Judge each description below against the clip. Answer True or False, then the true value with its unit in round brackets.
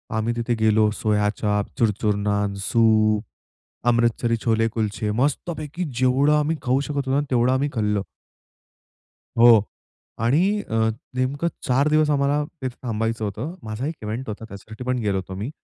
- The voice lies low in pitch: True (115 Hz)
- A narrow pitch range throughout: False (4.1 semitones)